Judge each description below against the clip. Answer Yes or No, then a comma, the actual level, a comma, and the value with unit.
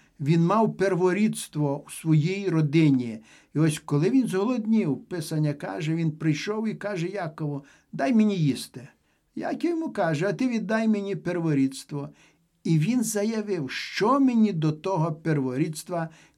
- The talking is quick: No, average, 135 wpm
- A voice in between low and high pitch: Yes, medium, 170 Hz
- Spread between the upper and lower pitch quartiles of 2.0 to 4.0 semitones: No, wide, 5.4 semitones